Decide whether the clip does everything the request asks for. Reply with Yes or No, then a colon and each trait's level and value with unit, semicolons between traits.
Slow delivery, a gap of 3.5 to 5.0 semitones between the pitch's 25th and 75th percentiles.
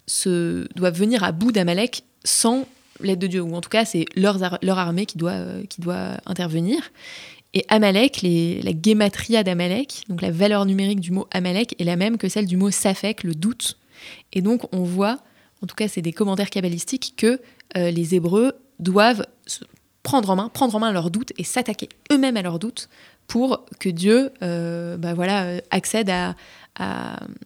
No: average, 190 wpm; average, 3.9 semitones